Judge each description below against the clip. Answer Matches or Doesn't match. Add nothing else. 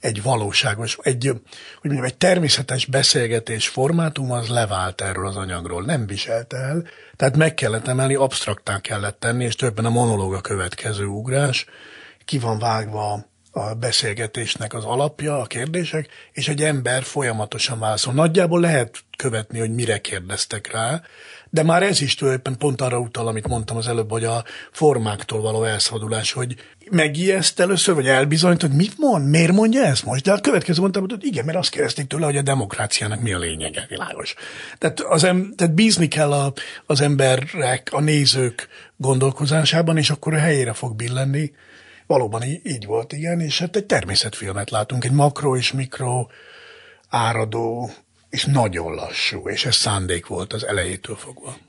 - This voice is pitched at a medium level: Doesn't match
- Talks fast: Matches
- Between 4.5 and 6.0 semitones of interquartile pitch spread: Matches